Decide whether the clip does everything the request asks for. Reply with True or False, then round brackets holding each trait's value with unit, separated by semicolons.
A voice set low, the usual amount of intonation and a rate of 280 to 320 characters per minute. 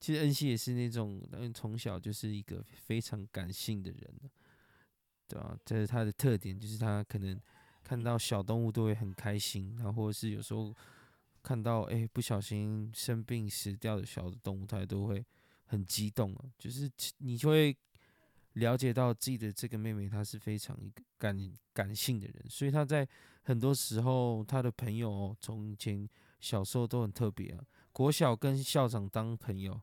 False (110 Hz; 3.1 semitones; 260 characters per minute)